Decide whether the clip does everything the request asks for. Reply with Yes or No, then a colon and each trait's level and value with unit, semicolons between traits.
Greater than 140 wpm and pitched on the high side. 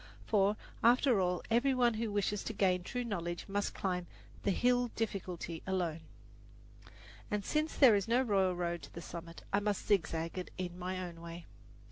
Yes: average, 175 wpm; high, 195 Hz